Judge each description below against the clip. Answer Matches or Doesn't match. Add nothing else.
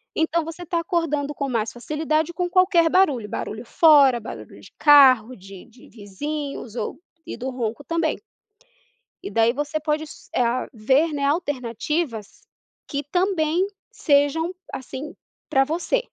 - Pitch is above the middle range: Matches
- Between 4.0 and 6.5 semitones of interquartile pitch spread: Matches